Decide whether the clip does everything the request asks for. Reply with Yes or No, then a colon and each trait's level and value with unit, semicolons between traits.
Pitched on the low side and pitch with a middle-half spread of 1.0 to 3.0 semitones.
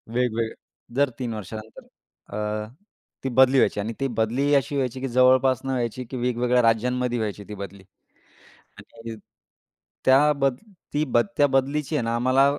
Yes: low, 125 Hz; average, 2.7 semitones